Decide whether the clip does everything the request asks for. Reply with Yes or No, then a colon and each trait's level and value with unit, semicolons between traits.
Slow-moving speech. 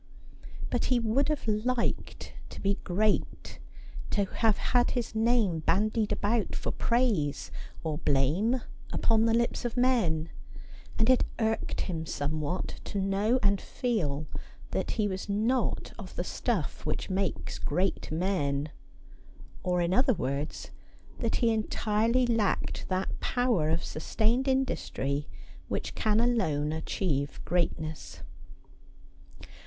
Yes: slow, 125 wpm